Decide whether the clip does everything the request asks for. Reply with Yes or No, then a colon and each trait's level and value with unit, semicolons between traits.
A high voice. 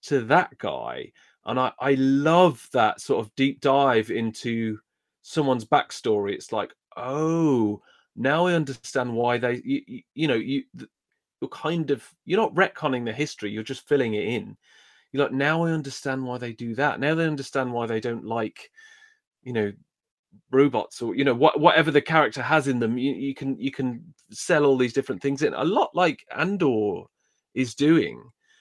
No: low, 135 Hz